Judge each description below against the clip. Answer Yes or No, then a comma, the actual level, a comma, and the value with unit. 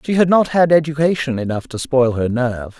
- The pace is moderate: No, fast, 215 wpm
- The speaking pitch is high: No, medium, 140 Hz